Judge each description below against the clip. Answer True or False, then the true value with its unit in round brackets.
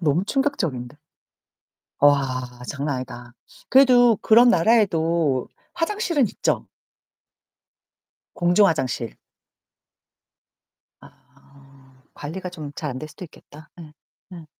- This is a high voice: False (155 Hz)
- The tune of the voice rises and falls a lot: True (7.3 semitones)